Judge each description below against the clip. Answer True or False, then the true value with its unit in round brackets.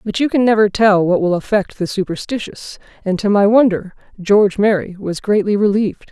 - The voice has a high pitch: True (200 Hz)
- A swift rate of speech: False (185 wpm)